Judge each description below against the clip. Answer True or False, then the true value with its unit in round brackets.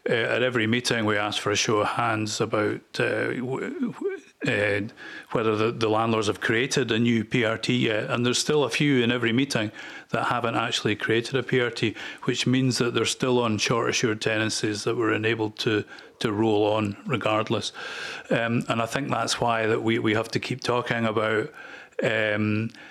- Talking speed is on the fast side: False (190 wpm)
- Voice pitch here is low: True (115 Hz)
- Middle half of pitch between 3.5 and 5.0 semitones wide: False (2.7 semitones)